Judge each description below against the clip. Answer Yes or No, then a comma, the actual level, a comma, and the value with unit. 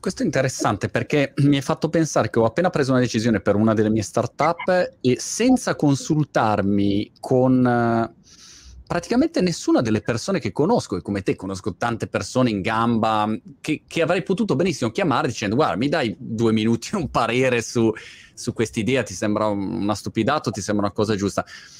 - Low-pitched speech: Yes, low, 120 Hz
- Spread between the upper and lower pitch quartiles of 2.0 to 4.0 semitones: No, wide, 5.5 semitones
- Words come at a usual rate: No, fast, 175 wpm